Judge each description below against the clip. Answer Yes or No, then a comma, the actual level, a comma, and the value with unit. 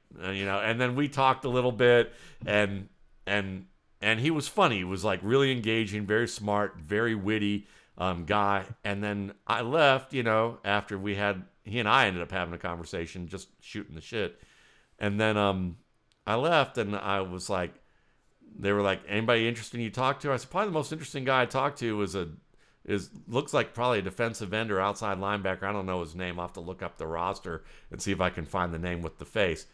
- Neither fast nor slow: No, fast, 220 wpm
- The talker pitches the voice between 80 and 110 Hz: Yes, low, 105 Hz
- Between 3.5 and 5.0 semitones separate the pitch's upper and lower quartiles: Yes, average, 3.8 semitones